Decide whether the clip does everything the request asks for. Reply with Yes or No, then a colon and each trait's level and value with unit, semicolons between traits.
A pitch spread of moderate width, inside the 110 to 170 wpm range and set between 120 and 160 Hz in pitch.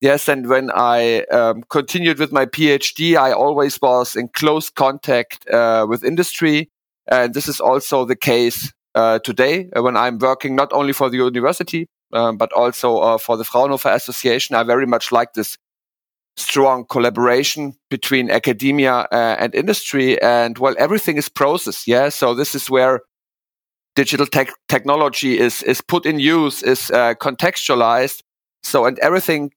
Yes: average, 3.2 semitones; average, 160 wpm; low, 135 Hz